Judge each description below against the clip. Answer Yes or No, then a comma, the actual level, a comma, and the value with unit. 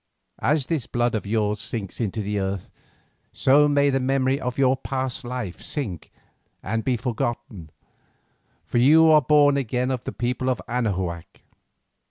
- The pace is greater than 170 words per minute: No, average, 155 wpm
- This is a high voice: No, low, 125 Hz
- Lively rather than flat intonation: No, average, 3.9 semitones